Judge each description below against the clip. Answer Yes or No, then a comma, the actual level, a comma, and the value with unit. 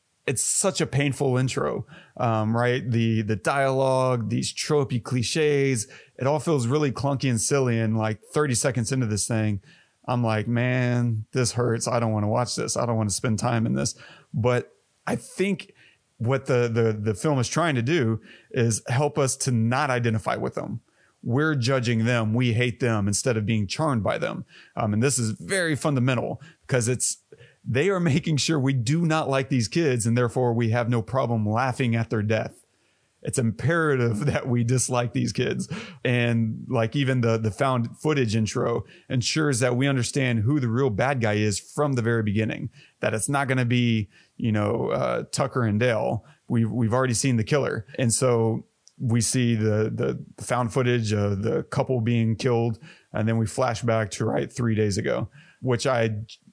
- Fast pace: No, average, 190 wpm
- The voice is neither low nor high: No, low, 125 Hz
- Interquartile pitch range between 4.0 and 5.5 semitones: No, average, 3.1 semitones